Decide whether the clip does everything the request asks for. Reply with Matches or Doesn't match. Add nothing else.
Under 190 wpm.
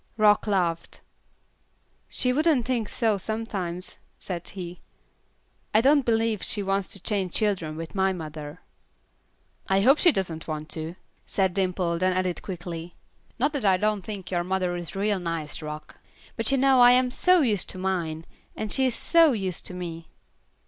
Matches